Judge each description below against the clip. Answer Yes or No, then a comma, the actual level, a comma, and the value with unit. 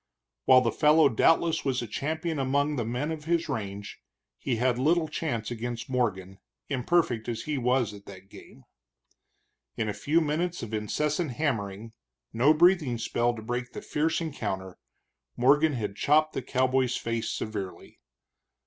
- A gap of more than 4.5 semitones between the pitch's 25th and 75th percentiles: Yes, average, 5.2 semitones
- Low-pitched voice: Yes, low, 125 Hz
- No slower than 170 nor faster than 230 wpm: No, average, 155 wpm